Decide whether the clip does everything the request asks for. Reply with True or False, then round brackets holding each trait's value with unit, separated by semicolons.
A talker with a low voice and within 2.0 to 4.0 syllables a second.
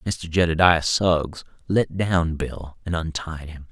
True (85 Hz; 3.7 syllables/s)